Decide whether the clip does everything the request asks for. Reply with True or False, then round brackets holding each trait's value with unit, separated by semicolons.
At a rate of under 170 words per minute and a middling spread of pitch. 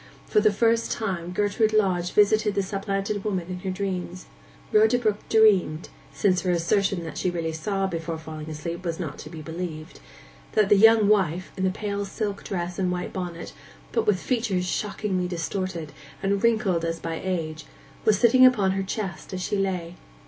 False (175 wpm; 3.4 semitones)